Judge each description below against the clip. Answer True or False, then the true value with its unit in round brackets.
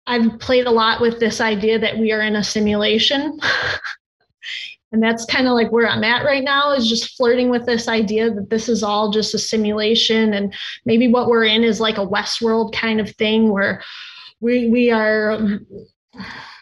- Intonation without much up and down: True (1.8 semitones)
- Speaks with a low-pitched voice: False (225 Hz)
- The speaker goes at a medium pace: True (190 wpm)